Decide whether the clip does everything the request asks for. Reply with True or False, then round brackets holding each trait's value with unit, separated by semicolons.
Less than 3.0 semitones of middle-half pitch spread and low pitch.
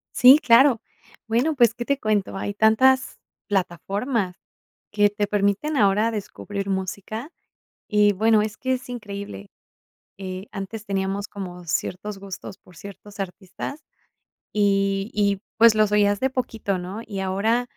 False (2.6 semitones; 205 Hz)